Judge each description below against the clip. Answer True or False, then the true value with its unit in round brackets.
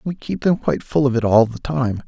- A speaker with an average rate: False (290 wpm)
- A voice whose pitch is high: False (125 Hz)